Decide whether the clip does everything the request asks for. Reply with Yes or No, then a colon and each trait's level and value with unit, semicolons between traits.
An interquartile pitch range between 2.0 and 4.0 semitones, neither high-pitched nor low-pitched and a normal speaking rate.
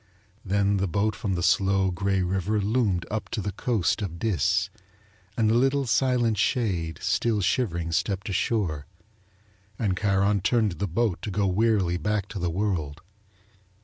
No: average, 3.1 semitones; low, 100 Hz; average, 155 wpm